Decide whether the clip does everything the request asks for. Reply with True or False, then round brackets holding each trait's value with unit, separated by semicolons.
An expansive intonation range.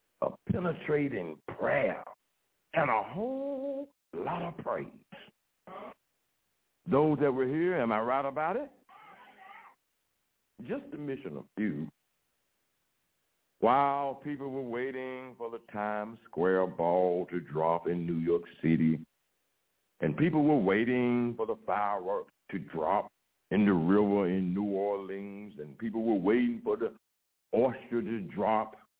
True (7.8 semitones)